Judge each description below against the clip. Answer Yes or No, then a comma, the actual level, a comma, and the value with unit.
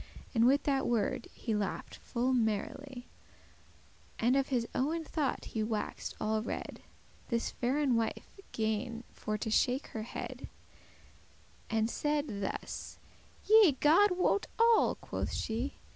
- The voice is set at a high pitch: Yes, high, 245 Hz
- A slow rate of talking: Yes, slow, 130 wpm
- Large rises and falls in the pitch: No, average, 4.4 semitones